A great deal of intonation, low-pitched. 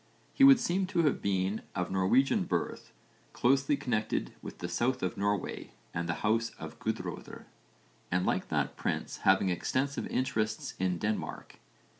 Yes: wide, 6.4 semitones; low, 110 Hz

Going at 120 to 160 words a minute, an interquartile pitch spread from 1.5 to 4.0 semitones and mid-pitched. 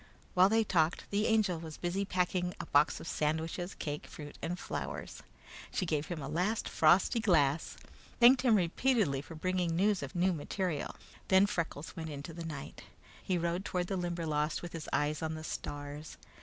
No: average, 180 wpm; average, 3.4 semitones; medium, 170 Hz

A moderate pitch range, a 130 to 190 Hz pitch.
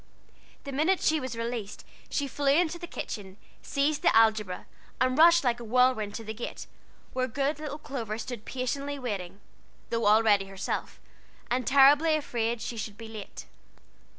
No: average, 4.5 semitones; high, 245 Hz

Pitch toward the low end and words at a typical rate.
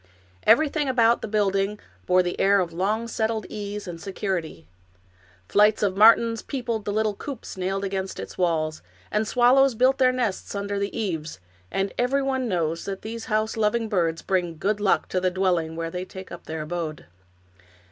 No: high, 200 Hz; average, 175 wpm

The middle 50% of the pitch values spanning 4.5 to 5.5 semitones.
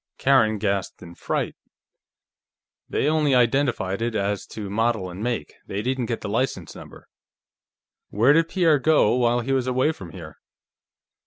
Yes: average, 4.9 semitones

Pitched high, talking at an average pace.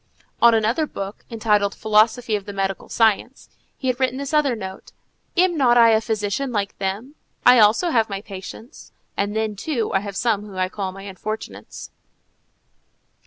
Yes: high, 220 Hz; average, 170 wpm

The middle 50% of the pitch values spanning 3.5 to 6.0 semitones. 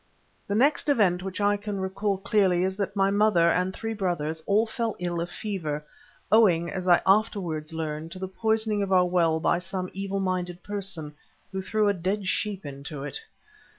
No: average, 2.9 semitones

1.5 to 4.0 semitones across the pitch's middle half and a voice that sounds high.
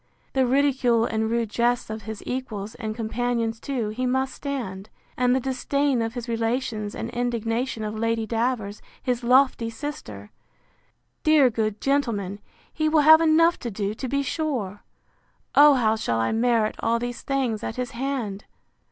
Yes: average, 3.2 semitones; high, 235 Hz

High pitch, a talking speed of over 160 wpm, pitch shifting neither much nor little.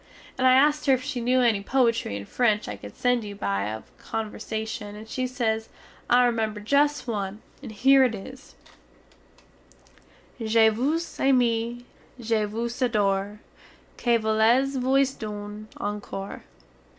No: high, 230 Hz; average, 145 wpm; average, 3.4 semitones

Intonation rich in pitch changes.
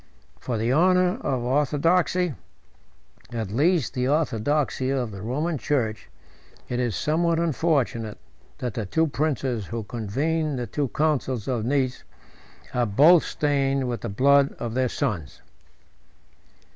No: average, 4.5 semitones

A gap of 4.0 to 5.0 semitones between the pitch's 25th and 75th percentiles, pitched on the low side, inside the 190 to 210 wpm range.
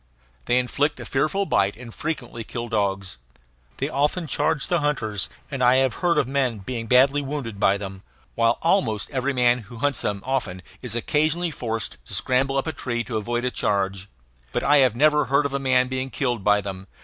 Yes: average, 4.3 semitones; low, 125 Hz; average, 200 wpm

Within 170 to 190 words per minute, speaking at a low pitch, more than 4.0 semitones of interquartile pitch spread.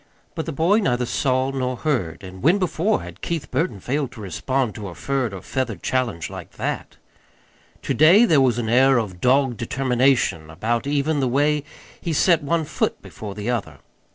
Yes: average, 185 wpm; low, 130 Hz; average, 4.4 semitones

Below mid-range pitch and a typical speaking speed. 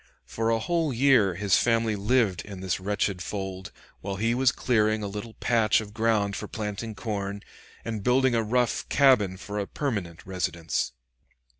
Yes: low, 105 Hz; average, 165 wpm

